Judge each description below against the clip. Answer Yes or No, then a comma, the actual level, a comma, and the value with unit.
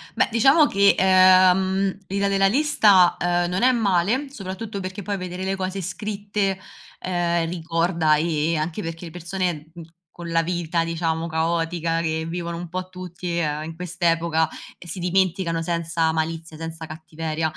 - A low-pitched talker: No, medium, 175 Hz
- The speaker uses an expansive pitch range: No, narrow, 2.4 semitones